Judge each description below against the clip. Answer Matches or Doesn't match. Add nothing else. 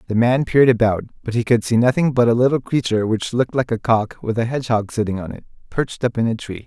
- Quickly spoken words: Matches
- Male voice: Matches